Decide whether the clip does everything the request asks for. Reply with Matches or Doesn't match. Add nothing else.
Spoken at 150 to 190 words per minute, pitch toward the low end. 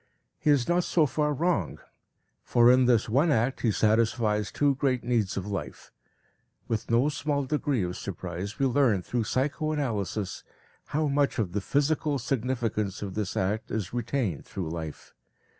Matches